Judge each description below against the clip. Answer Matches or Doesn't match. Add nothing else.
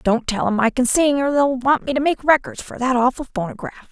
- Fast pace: Matches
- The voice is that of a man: Doesn't match